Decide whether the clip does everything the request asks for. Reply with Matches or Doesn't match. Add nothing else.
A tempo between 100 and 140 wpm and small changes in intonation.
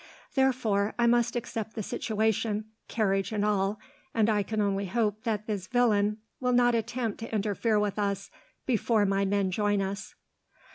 Doesn't match